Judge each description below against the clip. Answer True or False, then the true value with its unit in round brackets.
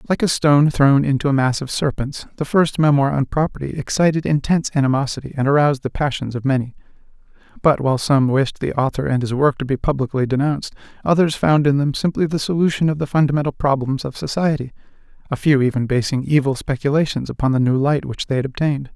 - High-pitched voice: False (140 Hz)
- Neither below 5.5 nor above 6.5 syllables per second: True (6.3 syllables/s)